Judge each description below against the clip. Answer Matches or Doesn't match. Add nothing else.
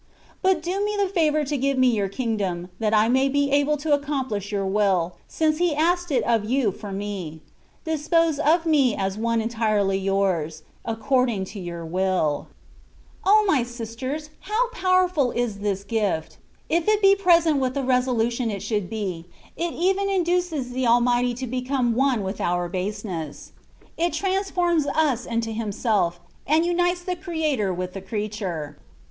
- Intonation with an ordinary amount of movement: Doesn't match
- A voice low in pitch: Doesn't match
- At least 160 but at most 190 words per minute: Matches